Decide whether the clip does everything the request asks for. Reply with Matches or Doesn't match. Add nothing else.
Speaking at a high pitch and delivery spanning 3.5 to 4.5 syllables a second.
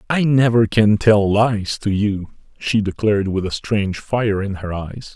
Doesn't match